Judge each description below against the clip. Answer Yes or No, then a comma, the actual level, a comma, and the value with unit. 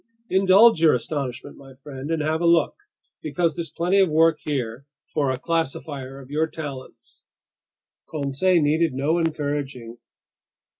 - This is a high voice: No, medium, 150 Hz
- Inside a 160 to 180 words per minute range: No, average, 140 wpm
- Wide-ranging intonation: No, average, 3.3 semitones